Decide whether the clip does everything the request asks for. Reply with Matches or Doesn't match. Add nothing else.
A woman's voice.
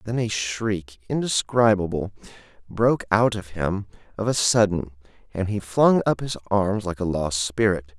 Doesn't match